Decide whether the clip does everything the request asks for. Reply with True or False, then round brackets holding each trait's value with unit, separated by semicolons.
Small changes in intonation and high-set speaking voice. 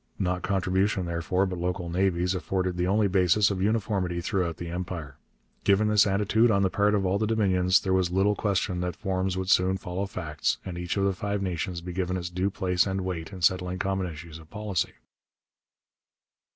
False (1.8 semitones; 95 Hz)